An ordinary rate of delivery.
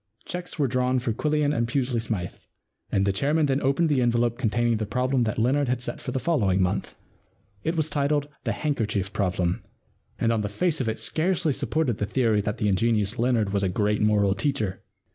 No: fast, 235 wpm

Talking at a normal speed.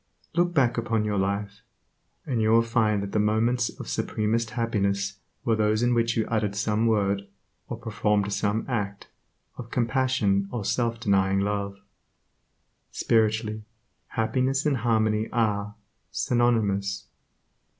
No: slow, 130 wpm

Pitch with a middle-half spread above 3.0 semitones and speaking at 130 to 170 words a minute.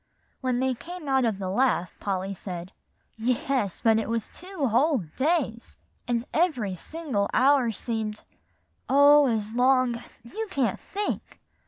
Yes: average, 4.6 semitones; average, 140 wpm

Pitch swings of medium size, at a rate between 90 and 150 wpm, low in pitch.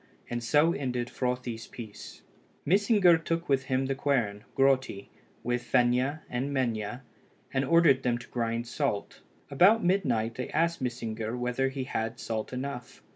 Yes: average, 3.0 semitones; average, 145 wpm; low, 125 Hz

